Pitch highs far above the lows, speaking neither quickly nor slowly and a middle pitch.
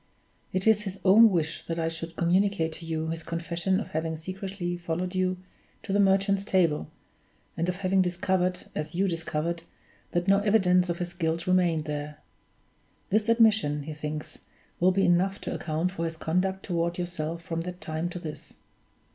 No: narrow, 2.6 semitones; average, 175 wpm; medium, 175 Hz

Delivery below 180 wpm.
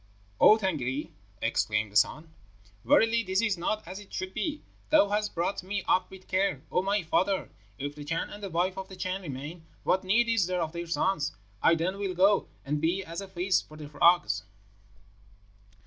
No: average, 195 wpm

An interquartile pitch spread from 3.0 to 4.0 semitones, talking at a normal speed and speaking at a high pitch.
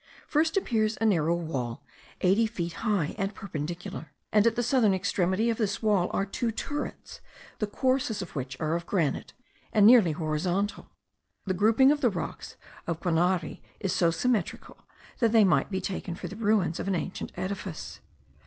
No: average, 4.4 semitones; average, 170 wpm; high, 195 Hz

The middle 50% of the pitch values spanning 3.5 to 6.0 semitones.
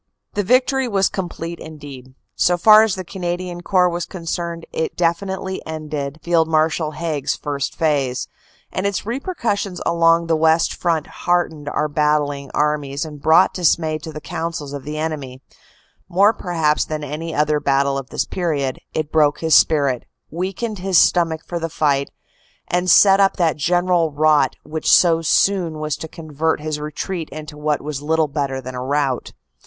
No: average, 2.9 semitones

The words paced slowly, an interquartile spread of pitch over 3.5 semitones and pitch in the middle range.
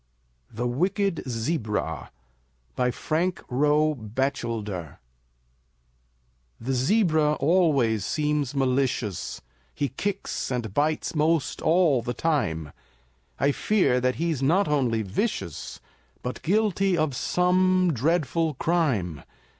Yes: slow, 100 wpm; wide, 5.6 semitones; medium, 145 Hz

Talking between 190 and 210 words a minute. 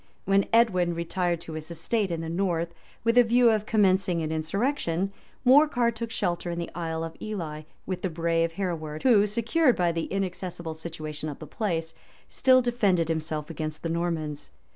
No: average, 175 wpm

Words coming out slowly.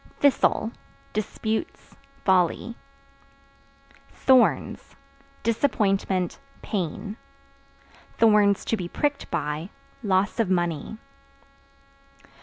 Yes: slow, 65 wpm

